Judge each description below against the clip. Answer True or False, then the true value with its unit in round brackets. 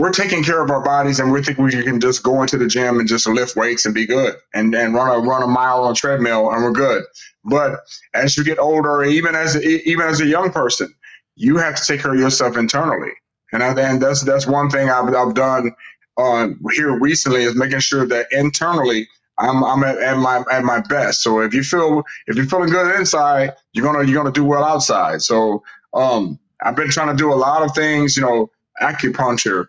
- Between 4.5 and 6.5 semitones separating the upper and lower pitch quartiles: False (3.1 semitones)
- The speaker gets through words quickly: True (230 wpm)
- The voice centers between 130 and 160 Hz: True (135 Hz)